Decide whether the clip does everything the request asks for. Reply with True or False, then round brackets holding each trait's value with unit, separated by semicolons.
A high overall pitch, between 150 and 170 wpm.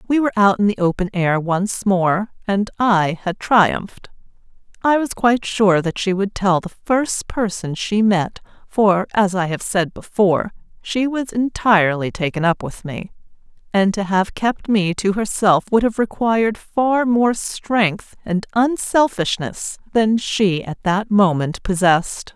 True (205 Hz; 160 wpm)